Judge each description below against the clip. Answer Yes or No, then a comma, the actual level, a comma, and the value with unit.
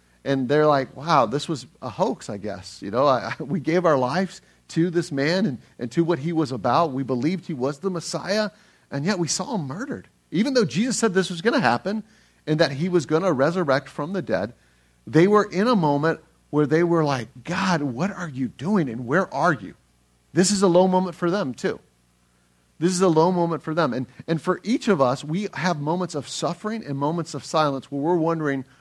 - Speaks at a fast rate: Yes, fast, 230 wpm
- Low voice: No, medium, 165 Hz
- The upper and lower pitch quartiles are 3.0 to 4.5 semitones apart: No, average, 5.3 semitones